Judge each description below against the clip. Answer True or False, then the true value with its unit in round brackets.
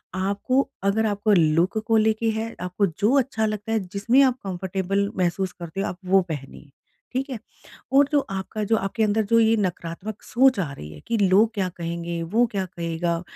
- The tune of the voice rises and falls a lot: False (3.8 semitones)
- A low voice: False (200 Hz)